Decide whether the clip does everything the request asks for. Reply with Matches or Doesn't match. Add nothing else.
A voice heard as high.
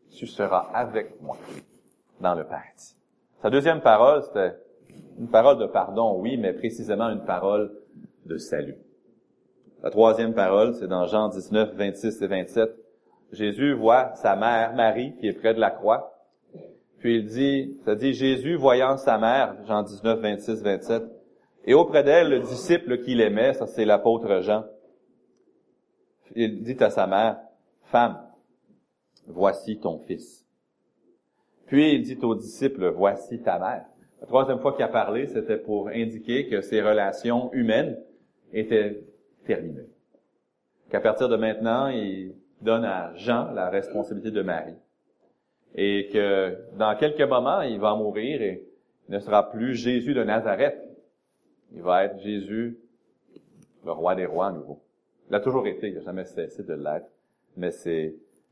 Doesn't match